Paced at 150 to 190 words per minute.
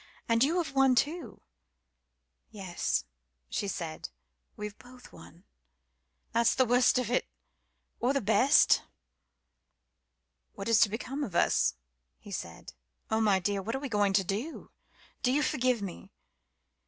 No: average, 140 wpm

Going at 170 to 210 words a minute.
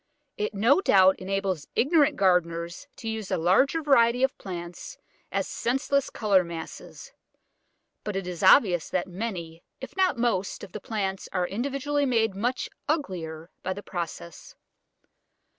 No: average, 140 wpm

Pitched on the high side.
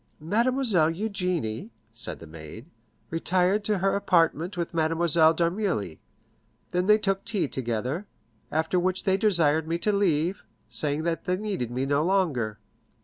No: medium, 170 Hz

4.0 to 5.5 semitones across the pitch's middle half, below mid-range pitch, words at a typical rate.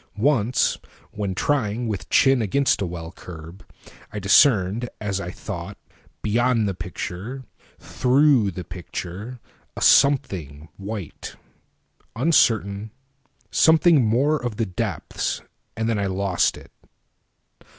No: average, 5.2 semitones; low, 105 Hz; slow, 100 wpm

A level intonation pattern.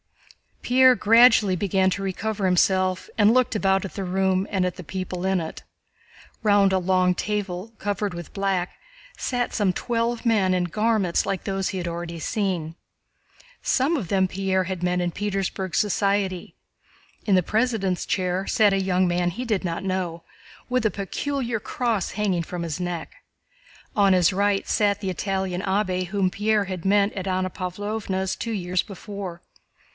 Yes: narrow, 2.3 semitones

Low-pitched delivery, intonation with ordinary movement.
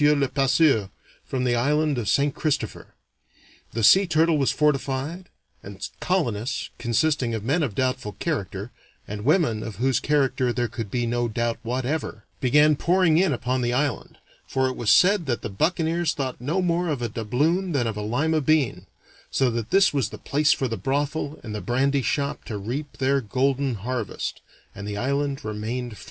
Yes: low, 130 Hz; average, 4.4 semitones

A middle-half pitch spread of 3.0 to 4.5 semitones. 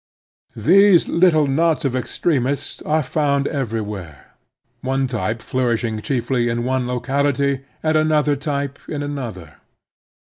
Yes: average, 3.6 semitones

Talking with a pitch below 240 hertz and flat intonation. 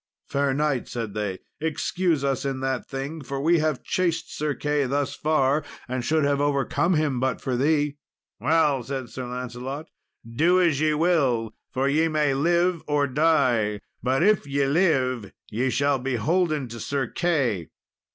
No: medium, 140 Hz; average, 3.3 semitones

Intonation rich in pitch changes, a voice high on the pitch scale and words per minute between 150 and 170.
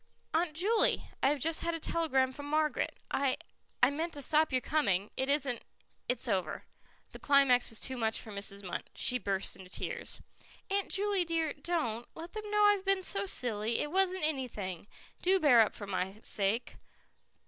No: wide, 7.0 semitones; very high, 280 Hz; average, 185 wpm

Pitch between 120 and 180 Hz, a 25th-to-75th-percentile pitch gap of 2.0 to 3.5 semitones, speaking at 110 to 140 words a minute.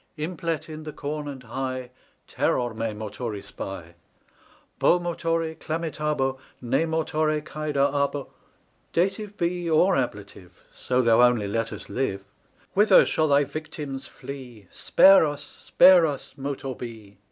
No: medium, 140 Hz; average, 4.8 semitones; slow, 135 wpm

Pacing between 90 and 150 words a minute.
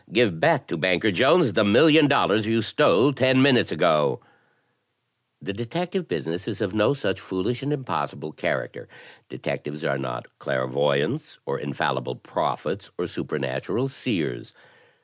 Yes: average, 140 wpm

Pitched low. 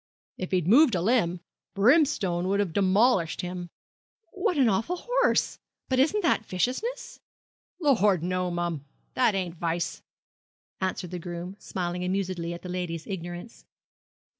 No: medium, 185 Hz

